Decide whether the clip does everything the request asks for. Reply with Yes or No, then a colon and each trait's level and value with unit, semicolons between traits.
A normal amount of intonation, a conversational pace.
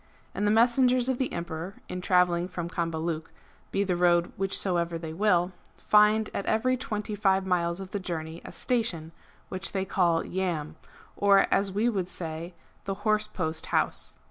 Yes: average, 3.5 semitones; average, 175 wpm